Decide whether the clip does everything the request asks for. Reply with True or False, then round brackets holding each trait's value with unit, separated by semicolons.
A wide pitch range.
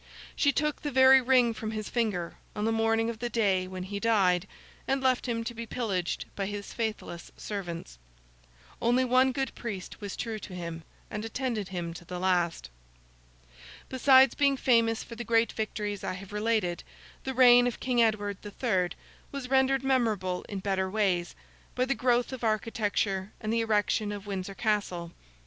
False (4.2 semitones)